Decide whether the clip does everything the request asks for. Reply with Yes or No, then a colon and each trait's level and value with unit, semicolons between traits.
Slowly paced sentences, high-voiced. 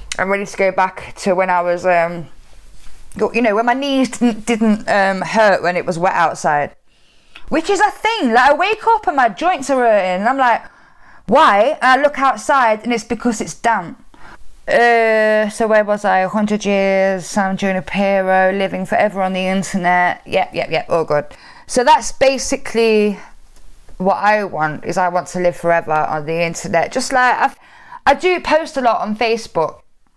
No: average, 195 wpm; high, 215 Hz